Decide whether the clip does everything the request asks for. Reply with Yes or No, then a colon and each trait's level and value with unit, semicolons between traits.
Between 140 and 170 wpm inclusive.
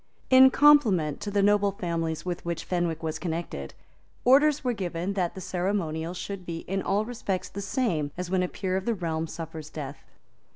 No: average, 190 wpm